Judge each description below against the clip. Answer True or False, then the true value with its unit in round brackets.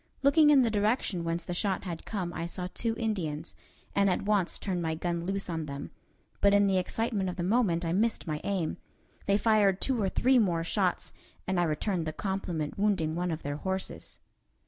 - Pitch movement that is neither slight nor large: True (3.6 semitones)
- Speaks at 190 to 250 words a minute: True (205 wpm)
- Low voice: False (190 Hz)